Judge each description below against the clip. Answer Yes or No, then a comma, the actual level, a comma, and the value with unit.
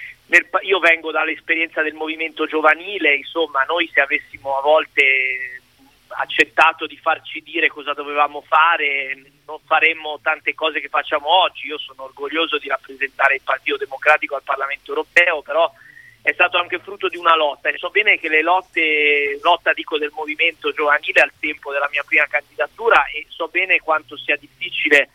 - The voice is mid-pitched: Yes, medium, 155 Hz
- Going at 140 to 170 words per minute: Yes, average, 165 wpm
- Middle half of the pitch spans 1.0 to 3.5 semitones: Yes, narrow, 2.6 semitones